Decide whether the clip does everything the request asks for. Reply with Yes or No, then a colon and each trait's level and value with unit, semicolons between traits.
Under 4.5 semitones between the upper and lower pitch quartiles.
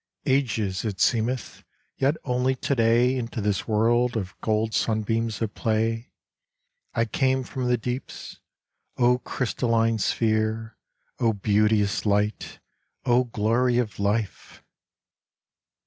Yes: narrow, 2.4 semitones